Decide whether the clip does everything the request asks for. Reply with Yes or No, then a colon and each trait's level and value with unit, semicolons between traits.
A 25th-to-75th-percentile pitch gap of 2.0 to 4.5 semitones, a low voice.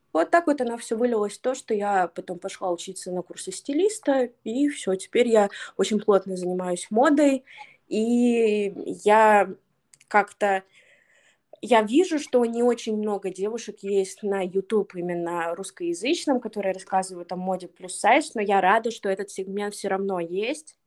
No: average, 4.2 semitones; high, 205 Hz